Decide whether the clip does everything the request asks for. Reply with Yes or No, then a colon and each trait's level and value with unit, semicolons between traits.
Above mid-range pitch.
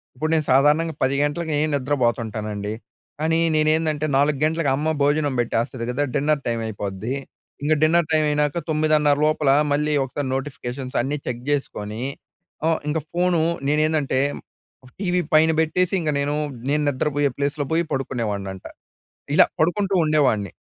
No: medium, 145 Hz